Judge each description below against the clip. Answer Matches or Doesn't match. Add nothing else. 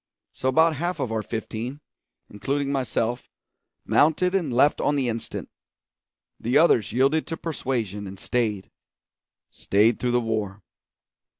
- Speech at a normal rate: Doesn't match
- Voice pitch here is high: Doesn't match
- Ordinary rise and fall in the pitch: Matches